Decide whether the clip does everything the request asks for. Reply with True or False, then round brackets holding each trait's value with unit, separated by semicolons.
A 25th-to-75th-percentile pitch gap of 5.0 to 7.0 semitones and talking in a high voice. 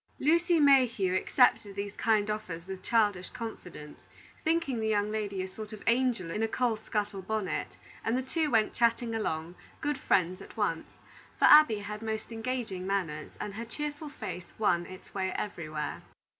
False (4.3 semitones; 215 Hz)